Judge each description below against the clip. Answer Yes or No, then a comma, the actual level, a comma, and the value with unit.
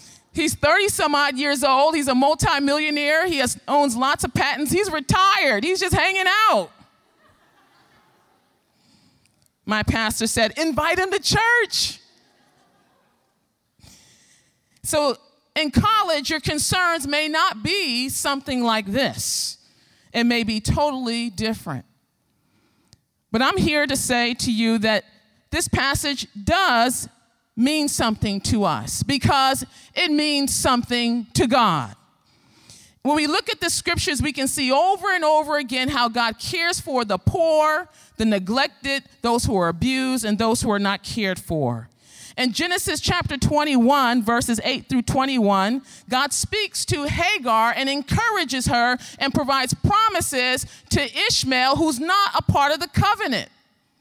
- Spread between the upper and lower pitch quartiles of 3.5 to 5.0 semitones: Yes, average, 4.7 semitones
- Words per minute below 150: Yes, average, 140 wpm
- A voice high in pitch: Yes, very high, 275 Hz